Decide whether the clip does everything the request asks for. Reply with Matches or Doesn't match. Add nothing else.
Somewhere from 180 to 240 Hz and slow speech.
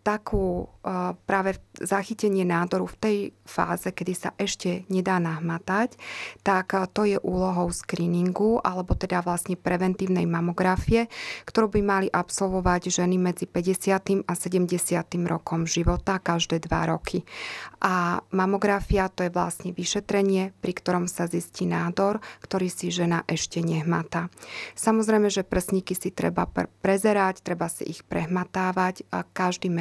Doesn't match